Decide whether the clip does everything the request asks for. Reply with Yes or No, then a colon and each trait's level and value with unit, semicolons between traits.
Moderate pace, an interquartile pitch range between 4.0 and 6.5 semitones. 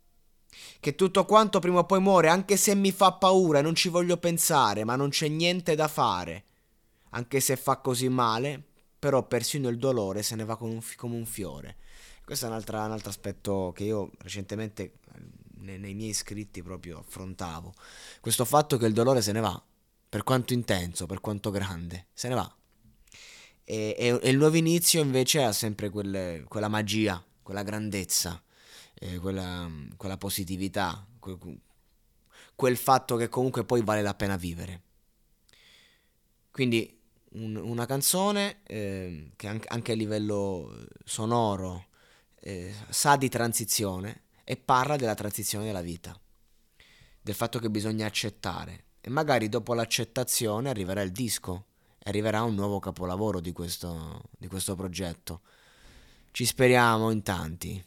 Yes: average, 145 wpm; average, 4.3 semitones